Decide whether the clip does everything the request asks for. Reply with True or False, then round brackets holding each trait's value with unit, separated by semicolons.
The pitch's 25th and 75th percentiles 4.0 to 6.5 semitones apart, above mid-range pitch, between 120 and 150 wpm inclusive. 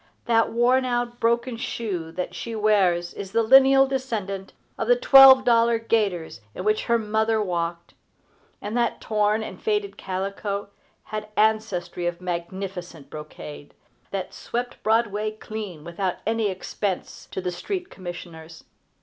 True (4.3 semitones; 215 Hz; 140 wpm)